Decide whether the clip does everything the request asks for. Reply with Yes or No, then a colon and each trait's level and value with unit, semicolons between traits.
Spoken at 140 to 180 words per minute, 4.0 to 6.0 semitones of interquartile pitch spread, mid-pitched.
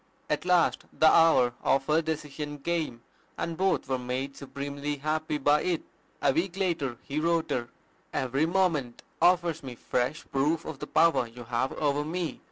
No: average, 170 wpm; average, 3.5 semitones; medium, 150 Hz